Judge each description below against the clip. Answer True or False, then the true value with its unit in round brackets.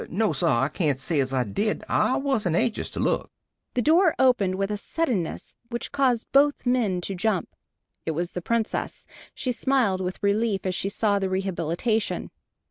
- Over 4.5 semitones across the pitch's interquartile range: True (5.3 semitones)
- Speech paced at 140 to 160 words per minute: False (180 wpm)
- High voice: True (200 Hz)